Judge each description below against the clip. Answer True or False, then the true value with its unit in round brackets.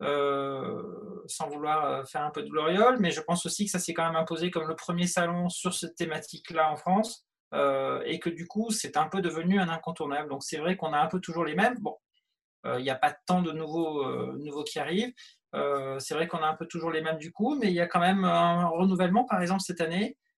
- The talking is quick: True (250 wpm)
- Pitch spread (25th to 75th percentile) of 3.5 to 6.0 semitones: False (3.0 semitones)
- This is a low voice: False (170 Hz)